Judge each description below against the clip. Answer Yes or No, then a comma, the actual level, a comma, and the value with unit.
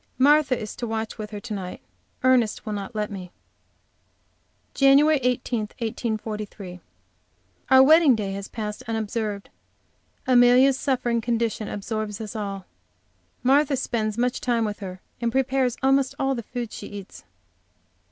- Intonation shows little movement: No, average, 3.5 semitones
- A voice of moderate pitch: No, high, 230 Hz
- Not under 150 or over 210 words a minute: No, average, 140 wpm